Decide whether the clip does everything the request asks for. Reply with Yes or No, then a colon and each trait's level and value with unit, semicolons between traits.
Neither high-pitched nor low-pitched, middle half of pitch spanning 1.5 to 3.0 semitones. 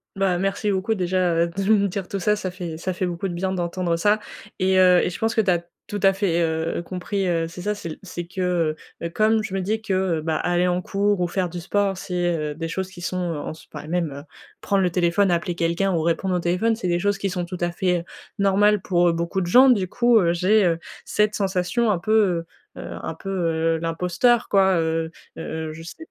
Yes: medium, 180 Hz; narrow, 2.6 semitones